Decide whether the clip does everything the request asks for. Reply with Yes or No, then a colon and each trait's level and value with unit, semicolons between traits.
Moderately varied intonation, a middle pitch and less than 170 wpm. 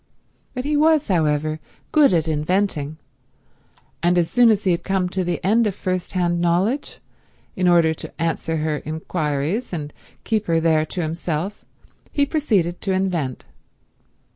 Yes: average, 4.1 semitones; medium, 175 Hz; average, 155 wpm